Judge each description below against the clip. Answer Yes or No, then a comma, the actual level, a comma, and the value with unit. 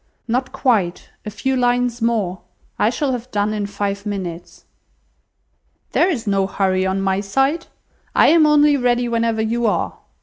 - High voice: Yes, high, 225 Hz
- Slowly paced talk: No, average, 160 wpm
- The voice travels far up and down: No, average, 4.0 semitones